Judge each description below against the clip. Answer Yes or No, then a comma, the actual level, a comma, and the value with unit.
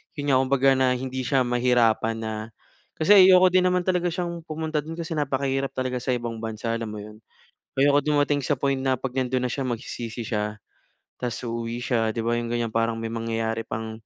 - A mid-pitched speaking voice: No, low, 125 Hz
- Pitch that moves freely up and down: No, average, 3.8 semitones